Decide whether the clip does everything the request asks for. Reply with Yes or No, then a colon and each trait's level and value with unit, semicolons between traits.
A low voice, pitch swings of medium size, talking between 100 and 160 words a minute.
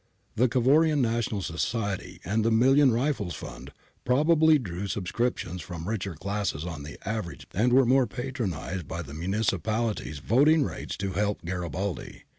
No: low, 105 Hz; wide, 5.7 semitones; average, 150 wpm